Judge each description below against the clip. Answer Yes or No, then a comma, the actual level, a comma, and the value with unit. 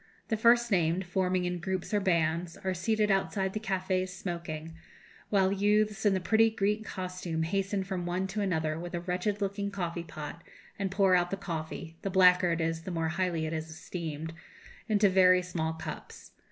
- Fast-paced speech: No, average, 185 wpm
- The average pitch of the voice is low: No, medium, 185 Hz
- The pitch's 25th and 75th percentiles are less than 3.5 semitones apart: Yes, average, 2.8 semitones